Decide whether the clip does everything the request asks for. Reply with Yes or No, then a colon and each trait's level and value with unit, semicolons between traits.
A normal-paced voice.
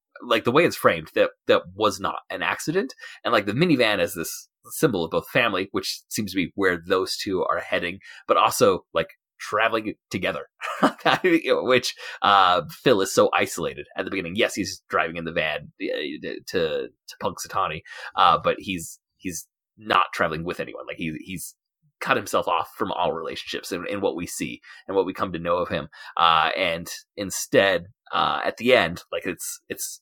Yes: average, 190 wpm